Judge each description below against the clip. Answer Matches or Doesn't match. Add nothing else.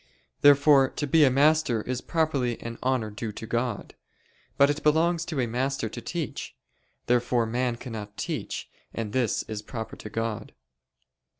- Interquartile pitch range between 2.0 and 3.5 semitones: Doesn't match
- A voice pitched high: Doesn't match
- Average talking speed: Matches